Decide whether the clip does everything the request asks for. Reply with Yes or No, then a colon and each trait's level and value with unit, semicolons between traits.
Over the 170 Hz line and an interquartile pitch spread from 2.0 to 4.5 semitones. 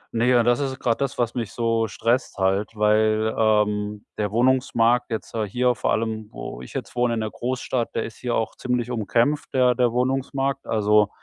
No: low, 115 Hz; narrow, 2.5 semitones